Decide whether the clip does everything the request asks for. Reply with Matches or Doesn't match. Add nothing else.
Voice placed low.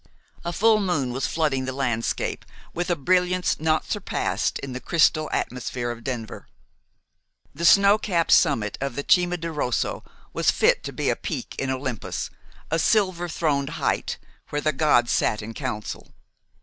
Doesn't match